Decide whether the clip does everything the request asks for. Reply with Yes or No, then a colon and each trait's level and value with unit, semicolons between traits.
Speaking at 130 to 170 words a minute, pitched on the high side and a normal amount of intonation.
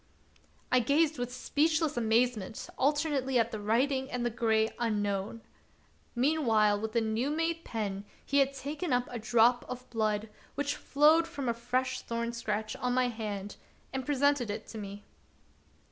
Yes: average, 160 wpm; high, 245 Hz; average, 4.1 semitones